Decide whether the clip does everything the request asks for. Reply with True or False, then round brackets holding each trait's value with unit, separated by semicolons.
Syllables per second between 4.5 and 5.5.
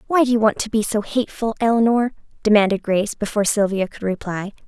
False (6.5 syllables/s)